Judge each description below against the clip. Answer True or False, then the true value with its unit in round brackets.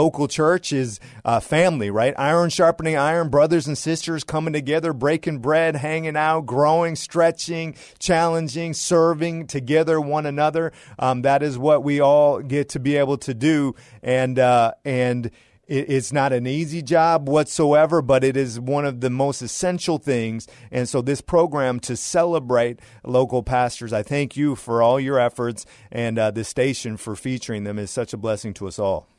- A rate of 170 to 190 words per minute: True (175 wpm)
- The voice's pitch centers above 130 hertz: True (140 Hz)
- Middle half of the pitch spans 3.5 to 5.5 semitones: True (4.2 semitones)